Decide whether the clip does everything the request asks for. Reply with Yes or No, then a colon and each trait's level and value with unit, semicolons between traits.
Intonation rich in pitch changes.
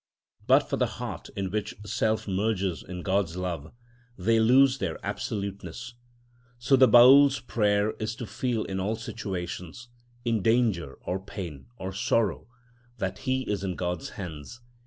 No: average, 4.3 semitones